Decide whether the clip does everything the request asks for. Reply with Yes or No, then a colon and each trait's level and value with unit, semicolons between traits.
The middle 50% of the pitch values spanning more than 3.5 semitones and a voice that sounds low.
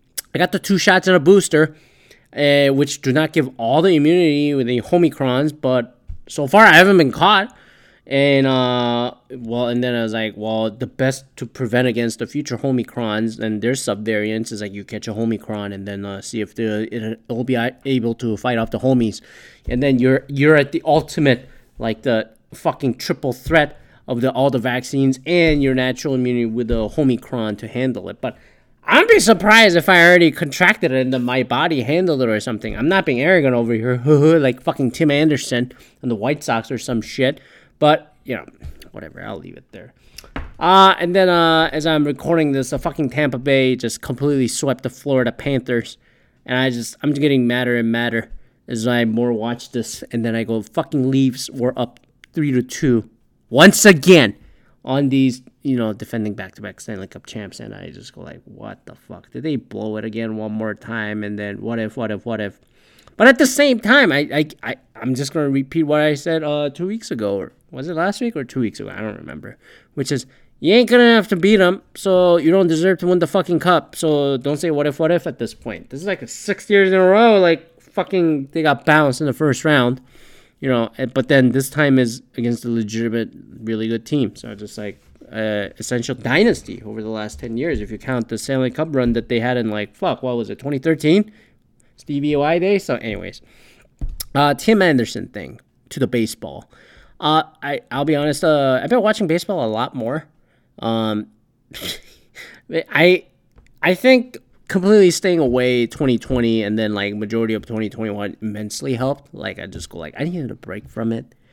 Yes: average, 5.1 semitones; low, 130 Hz